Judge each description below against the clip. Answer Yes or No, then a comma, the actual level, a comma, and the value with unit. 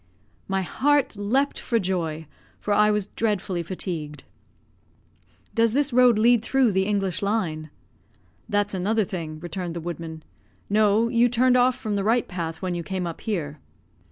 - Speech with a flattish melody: No, average, 4.7 semitones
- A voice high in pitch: Yes, high, 200 Hz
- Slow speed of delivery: No, average, 155 wpm